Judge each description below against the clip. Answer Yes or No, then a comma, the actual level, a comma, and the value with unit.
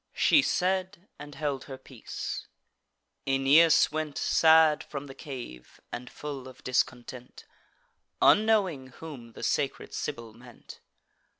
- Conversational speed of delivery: No, slow, 115 wpm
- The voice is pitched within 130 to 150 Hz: Yes, medium, 140 Hz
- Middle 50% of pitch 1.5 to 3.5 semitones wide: No, average, 4.1 semitones